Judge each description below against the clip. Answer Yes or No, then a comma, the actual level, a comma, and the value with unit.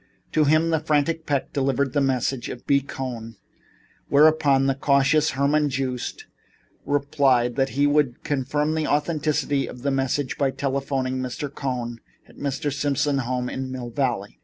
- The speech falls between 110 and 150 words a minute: No, average, 160 wpm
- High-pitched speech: No, medium, 140 Hz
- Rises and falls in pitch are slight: Yes, narrow, 2.1 semitones